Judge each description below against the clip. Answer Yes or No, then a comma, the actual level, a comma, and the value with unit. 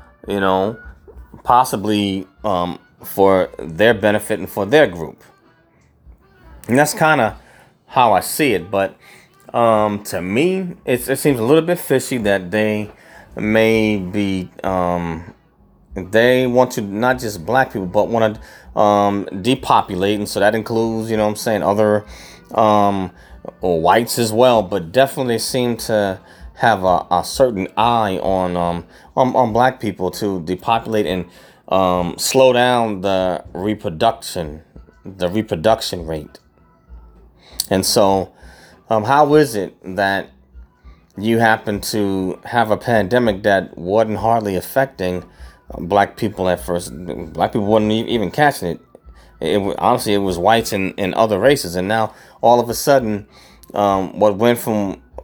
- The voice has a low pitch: Yes, low, 105 Hz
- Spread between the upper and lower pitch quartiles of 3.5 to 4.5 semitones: Yes, average, 3.8 semitones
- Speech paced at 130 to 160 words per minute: Yes, average, 145 wpm